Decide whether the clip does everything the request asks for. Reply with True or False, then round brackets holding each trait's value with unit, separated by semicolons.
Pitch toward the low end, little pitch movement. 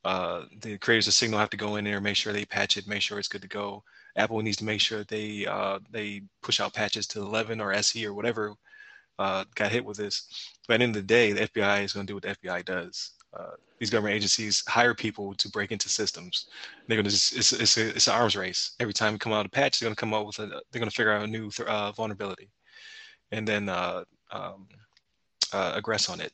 True (105 Hz; 1.3 semitones)